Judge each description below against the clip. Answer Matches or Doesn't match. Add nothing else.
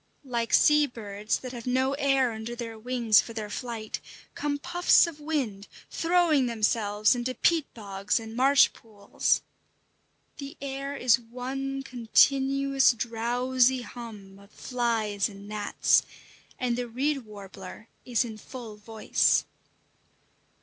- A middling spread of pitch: Matches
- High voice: Matches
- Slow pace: Matches